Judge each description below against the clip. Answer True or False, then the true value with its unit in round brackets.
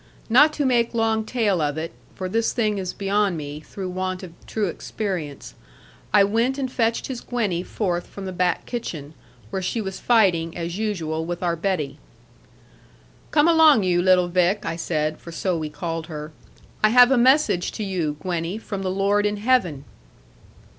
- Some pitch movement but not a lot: True (4.7 semitones)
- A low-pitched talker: False (190 Hz)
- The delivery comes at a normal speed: True (180 wpm)